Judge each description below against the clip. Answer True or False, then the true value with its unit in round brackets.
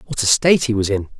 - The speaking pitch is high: False (120 Hz)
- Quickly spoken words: True (305 wpm)